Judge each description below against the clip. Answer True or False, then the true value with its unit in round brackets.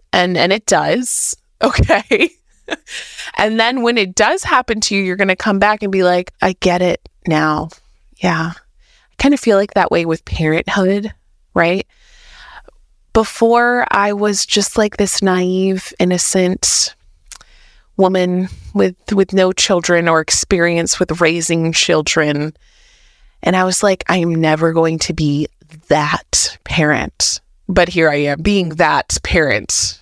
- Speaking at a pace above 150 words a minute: False (145 wpm)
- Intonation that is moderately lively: True (4.2 semitones)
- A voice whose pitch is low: False (185 Hz)